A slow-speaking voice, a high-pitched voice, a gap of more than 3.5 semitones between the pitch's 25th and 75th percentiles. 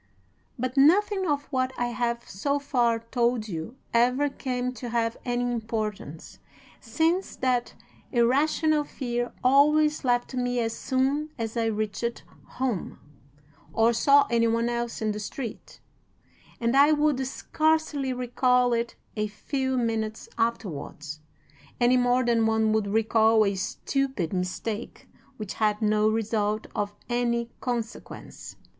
No: slow, 130 wpm; high, 240 Hz; average, 2.9 semitones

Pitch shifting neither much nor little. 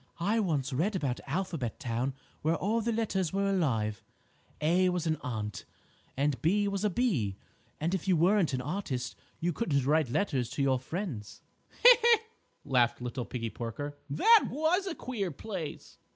No: wide, 7.6 semitones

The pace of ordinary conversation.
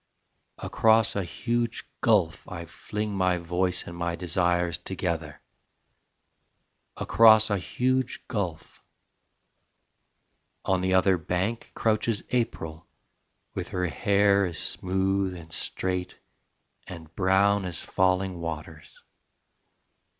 No: slow, 100 wpm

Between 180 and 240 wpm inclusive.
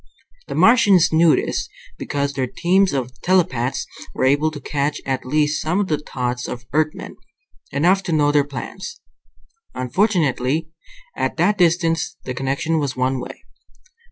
No: average, 150 wpm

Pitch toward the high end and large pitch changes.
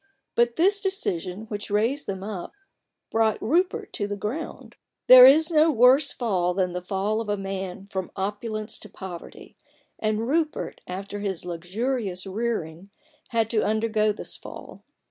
No: high, 215 Hz; average, 3.8 semitones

